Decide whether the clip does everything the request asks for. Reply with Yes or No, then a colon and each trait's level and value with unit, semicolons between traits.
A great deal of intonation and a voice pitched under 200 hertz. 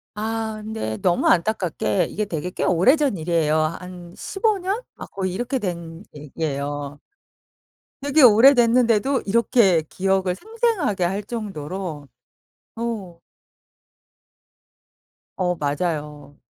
Yes: wide, 5.9 semitones; high, 190 Hz